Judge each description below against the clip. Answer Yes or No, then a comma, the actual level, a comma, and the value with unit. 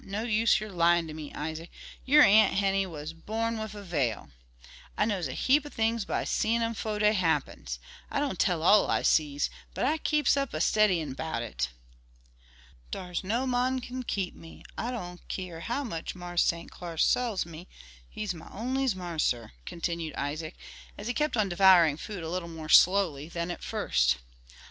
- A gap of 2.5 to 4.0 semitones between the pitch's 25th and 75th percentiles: No, wide, 5.4 semitones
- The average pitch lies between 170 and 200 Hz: Yes, medium, 185 Hz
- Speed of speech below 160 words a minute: No, average, 185 wpm